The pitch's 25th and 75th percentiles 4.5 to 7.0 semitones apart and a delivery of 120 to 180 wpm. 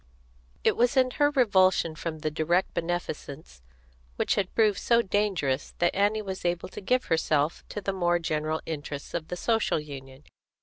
Yes: average, 4.8 semitones; average, 170 wpm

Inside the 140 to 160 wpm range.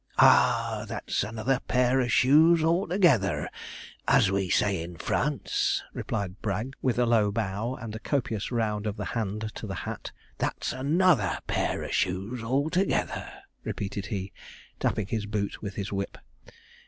Yes: average, 150 wpm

